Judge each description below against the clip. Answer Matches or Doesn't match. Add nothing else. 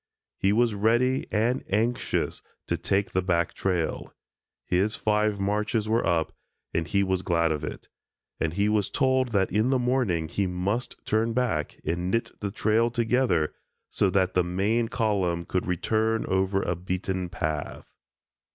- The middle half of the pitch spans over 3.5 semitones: Matches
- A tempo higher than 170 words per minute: Doesn't match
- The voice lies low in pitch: Matches